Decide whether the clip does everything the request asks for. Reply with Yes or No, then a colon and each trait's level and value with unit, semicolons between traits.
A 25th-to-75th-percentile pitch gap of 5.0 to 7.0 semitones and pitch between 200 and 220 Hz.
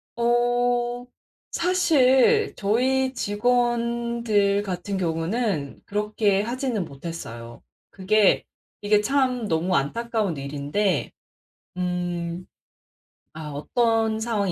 Yes: average, 5.3 semitones; high, 210 Hz